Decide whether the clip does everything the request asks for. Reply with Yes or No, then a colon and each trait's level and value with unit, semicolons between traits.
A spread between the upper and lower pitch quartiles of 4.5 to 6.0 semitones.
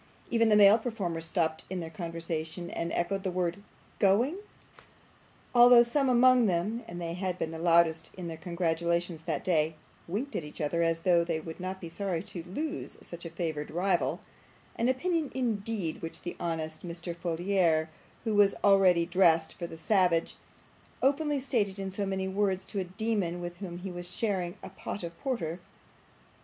No: average, 3.5 semitones